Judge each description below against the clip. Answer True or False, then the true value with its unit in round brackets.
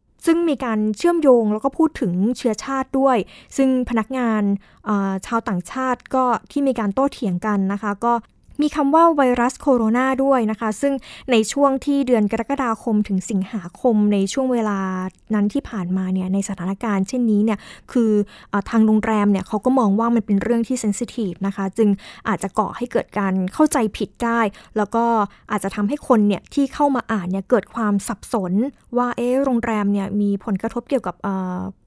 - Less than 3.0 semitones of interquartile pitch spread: False (4.0 semitones)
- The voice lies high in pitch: True (225 Hz)